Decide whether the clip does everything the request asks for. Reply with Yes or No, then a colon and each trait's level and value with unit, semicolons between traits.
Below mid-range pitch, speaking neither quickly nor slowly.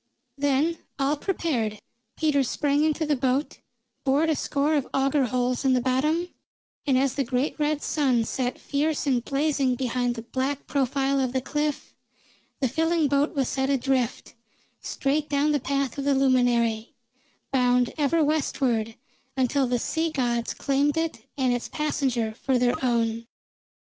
No: very high, 270 Hz; average, 155 wpm